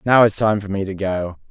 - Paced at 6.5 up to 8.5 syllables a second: No, 5.4 syllables/s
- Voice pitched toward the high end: No, low, 100 Hz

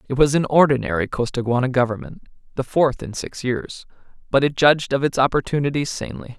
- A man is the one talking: Yes, male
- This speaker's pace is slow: No, average, 150 wpm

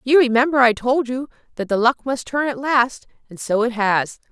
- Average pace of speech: No, fast, 225 wpm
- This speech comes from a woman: Yes, female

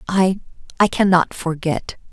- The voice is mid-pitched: Yes, medium, 180 Hz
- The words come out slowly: Yes, slow, 85 wpm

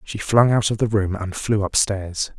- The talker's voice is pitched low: Yes, low, 105 Hz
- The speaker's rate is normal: No, fast, 225 wpm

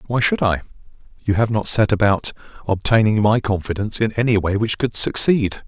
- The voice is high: No, low, 105 Hz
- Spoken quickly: No, average, 180 wpm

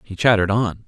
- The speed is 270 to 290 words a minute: No, fast, 205 wpm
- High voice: No, low, 105 Hz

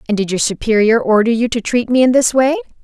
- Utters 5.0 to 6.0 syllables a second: No, 6.2 syllables/s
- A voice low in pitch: No, high, 225 Hz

